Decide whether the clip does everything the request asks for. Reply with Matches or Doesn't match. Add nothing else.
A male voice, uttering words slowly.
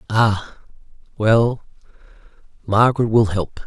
Matches